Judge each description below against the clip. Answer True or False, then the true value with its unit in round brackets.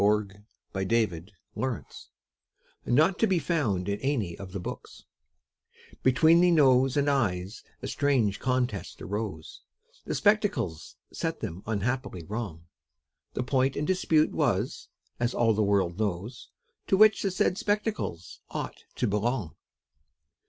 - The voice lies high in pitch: False (120 Hz)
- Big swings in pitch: True (6.5 semitones)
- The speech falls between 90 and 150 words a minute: True (140 wpm)